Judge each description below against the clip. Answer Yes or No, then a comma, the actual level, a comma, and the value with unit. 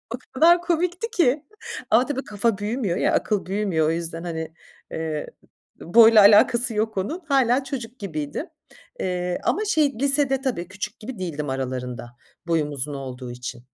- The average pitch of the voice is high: Yes, high, 205 Hz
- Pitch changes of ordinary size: No, wide, 8.4 semitones